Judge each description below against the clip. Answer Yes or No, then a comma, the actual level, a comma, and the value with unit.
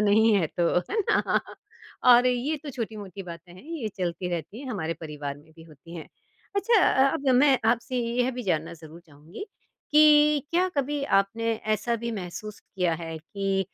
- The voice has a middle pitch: No, high, 210 Hz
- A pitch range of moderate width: No, wide, 7.1 semitones